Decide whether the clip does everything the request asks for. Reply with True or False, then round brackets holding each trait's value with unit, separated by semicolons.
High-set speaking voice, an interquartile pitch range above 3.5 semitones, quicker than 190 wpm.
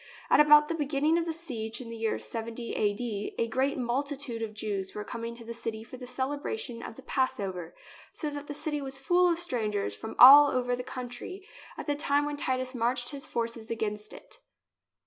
True (250 Hz; 4.2 semitones; 205 wpm)